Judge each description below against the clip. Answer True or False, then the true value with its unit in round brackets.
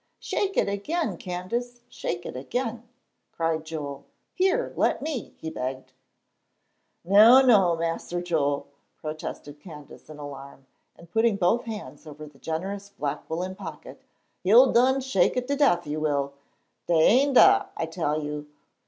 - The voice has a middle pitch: True (175 Hz)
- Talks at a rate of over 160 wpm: False (145 wpm)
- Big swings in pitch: True (7.9 semitones)